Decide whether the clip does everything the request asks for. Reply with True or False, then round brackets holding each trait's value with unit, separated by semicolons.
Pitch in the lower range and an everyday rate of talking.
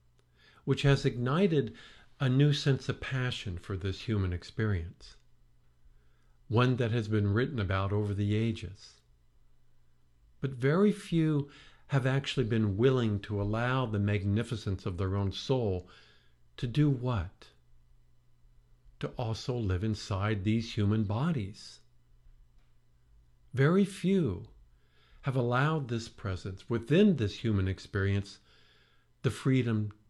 False (105 Hz; 115 wpm)